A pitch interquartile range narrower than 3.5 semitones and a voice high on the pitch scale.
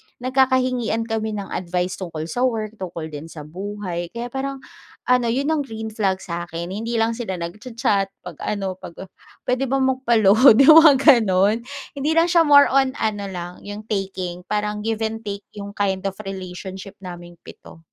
No: average, 4.7 semitones; high, 210 Hz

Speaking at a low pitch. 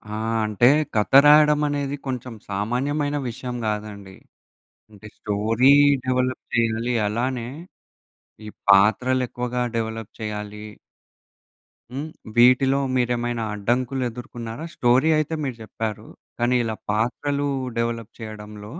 Yes: low, 120 Hz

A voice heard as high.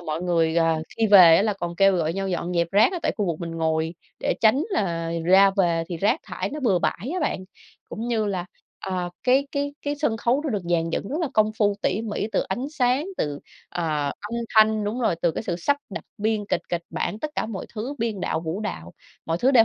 Yes: high, 195 Hz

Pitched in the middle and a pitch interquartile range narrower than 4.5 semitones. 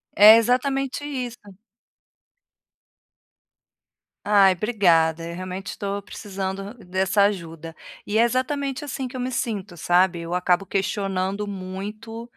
No: high, 200 Hz; average, 4.1 semitones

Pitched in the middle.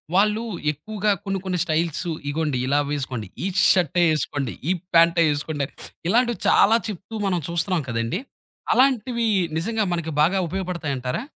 Yes: medium, 175 Hz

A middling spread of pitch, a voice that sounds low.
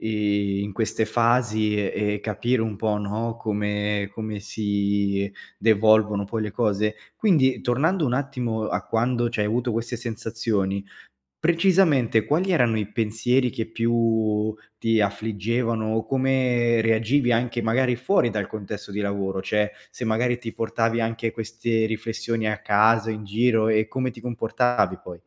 No: narrow, 2.2 semitones; low, 110 Hz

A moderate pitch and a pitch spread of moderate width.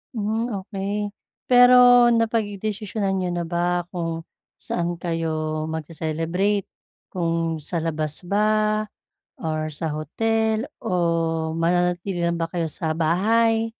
Yes: medium, 175 Hz; average, 4.5 semitones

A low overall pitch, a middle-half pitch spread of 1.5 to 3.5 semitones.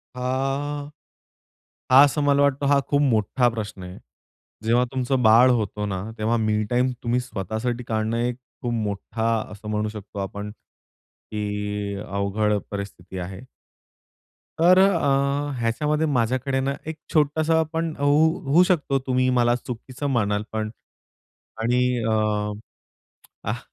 No: low, 120 Hz; average, 4.7 semitones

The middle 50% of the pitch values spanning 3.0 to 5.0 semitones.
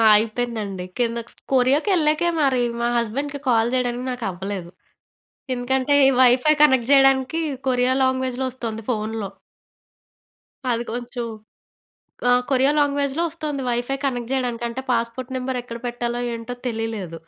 No: narrow, 2.4 semitones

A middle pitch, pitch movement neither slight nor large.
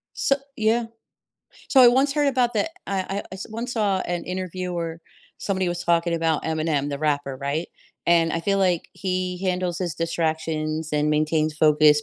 Yes: medium, 175 Hz; average, 3.8 semitones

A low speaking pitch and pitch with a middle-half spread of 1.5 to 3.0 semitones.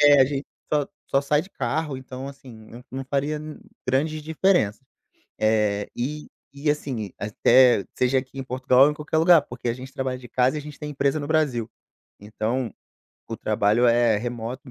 No: low, 130 Hz; average, 3.6 semitones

